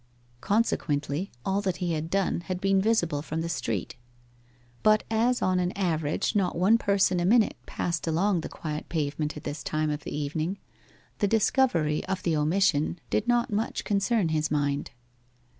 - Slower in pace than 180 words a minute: Yes, average, 170 wpm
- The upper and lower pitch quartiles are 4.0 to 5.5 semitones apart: Yes, average, 4.6 semitones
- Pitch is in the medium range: Yes, medium, 175 Hz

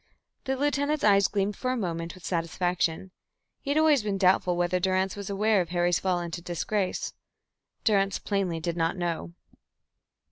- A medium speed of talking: Yes, average, 165 wpm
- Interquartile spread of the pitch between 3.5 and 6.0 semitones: No, average, 3.1 semitones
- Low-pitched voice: No, medium, 185 Hz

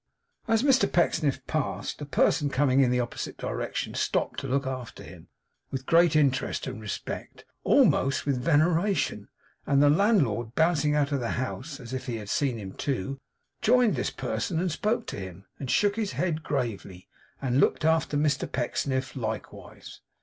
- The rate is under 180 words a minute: Yes, average, 170 wpm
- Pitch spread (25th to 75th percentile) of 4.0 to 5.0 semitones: Yes, average, 4.3 semitones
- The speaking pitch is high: No, medium, 140 Hz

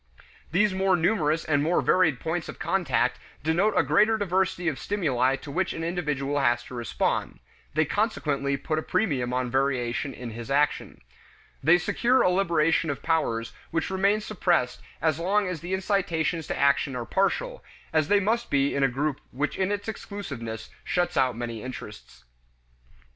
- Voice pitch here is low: No, medium, 160 Hz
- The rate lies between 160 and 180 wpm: Yes, average, 170 wpm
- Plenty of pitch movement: Yes, wide, 5.7 semitones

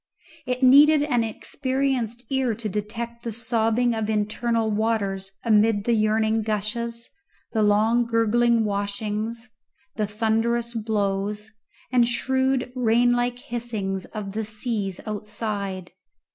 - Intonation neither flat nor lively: No, narrow, 2.3 semitones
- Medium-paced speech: No, slow, 115 wpm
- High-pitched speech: Yes, high, 225 Hz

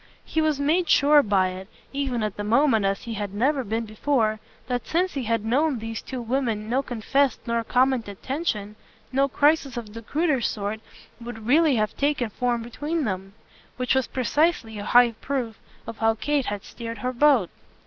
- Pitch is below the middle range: No, high, 240 Hz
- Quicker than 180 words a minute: Yes, average, 190 wpm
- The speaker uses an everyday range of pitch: Yes, average, 4.3 semitones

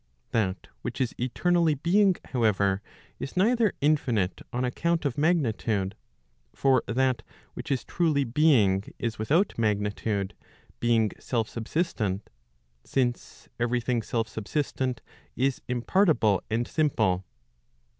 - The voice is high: No, low, 120 Hz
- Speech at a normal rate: No, slow, 115 wpm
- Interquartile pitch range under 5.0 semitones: No, wide, 5.4 semitones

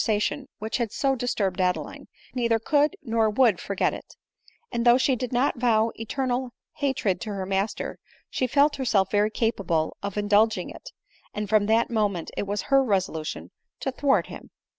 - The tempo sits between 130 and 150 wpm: No, average, 180 wpm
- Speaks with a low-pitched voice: No, high, 225 Hz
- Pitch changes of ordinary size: Yes, average, 4.0 semitones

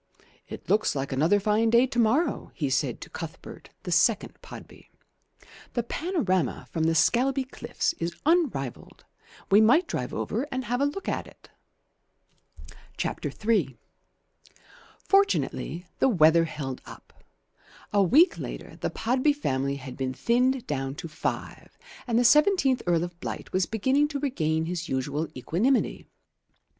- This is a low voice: No, high, 220 Hz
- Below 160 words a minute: Yes, average, 145 wpm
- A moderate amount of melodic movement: No, wide, 8.7 semitones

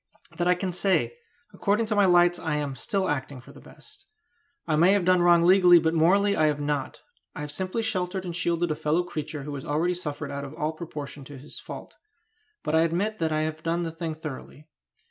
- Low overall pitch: No, medium, 165 Hz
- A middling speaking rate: No, fast, 220 wpm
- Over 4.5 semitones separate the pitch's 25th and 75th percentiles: No, average, 3.1 semitones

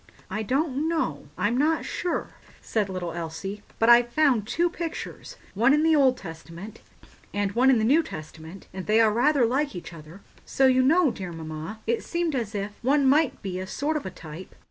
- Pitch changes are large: Yes, wide, 7.3 semitones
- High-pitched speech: Yes, high, 230 Hz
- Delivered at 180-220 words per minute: Yes, average, 190 wpm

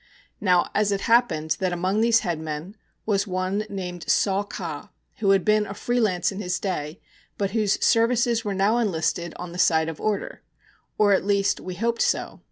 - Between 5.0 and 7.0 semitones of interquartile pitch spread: No, average, 3.1 semitones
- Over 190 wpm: No, average, 180 wpm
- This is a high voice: Yes, high, 195 Hz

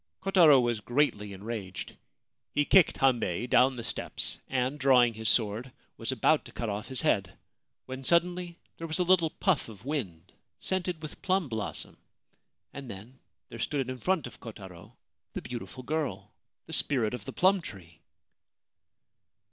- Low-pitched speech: Yes, low, 130 Hz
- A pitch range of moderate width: No, wide, 6.1 semitones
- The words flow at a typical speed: Yes, average, 155 wpm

